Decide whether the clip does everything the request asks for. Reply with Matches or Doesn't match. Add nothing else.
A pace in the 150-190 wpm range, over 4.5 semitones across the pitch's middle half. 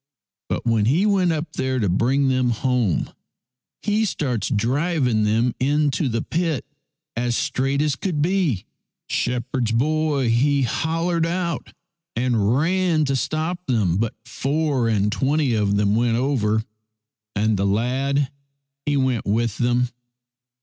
Doesn't match